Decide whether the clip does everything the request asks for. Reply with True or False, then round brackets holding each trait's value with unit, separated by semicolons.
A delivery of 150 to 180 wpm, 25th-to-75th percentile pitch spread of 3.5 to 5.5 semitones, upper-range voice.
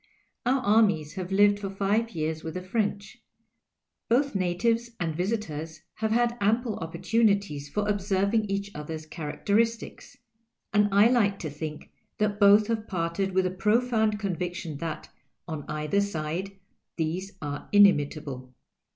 False (140 wpm; 4.6 semitones; 195 Hz)